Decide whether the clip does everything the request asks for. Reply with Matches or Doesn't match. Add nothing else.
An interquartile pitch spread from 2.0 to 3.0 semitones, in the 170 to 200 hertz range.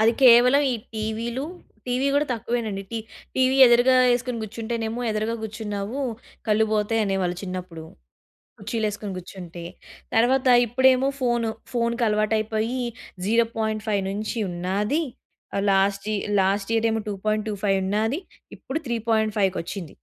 Doesn't match